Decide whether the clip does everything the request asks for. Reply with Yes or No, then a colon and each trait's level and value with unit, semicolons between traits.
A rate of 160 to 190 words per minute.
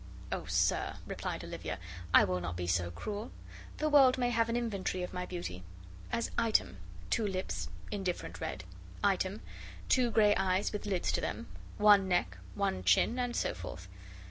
Yes: average, 170 wpm